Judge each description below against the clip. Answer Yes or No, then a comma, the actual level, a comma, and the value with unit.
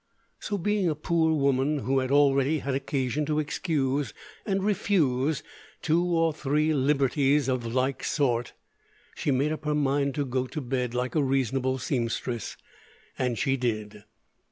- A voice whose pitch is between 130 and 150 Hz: Yes, medium, 140 Hz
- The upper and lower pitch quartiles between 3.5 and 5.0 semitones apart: No, average, 3.0 semitones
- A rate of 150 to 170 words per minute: Yes, average, 155 wpm